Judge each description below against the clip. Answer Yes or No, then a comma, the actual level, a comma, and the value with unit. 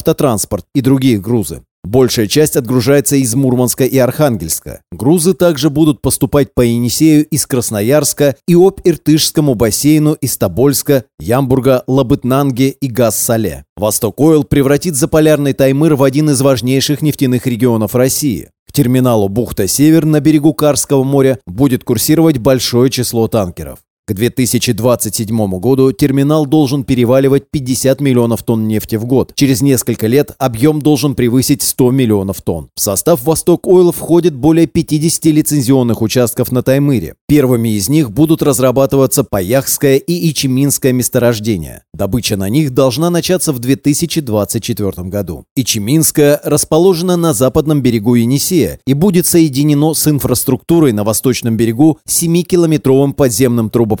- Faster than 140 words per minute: No, average, 130 wpm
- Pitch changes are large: No, average, 4.1 semitones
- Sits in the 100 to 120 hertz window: No, low, 135 Hz